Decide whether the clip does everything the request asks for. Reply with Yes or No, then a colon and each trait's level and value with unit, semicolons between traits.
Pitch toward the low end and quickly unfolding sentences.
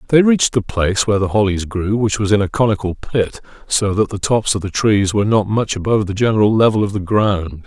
Yes: low, 105 Hz; fast, 245 wpm